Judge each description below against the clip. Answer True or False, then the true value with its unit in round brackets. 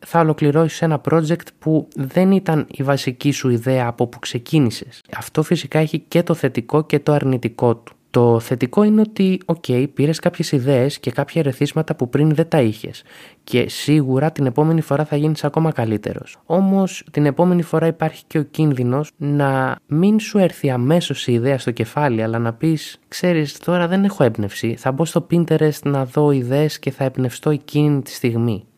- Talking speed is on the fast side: True (185 wpm)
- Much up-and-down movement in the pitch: False (3.7 semitones)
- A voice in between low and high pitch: True (150 Hz)